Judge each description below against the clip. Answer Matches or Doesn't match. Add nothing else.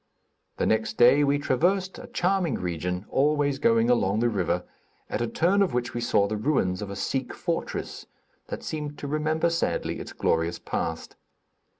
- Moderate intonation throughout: Doesn't match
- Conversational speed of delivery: Matches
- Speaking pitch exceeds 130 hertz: Doesn't match